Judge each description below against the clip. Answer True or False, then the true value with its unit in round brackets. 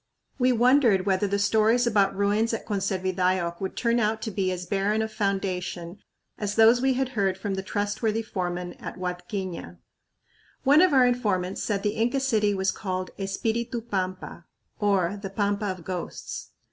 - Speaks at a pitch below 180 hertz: False (200 Hz)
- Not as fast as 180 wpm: True (165 wpm)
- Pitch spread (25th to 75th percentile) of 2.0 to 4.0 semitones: True (3.1 semitones)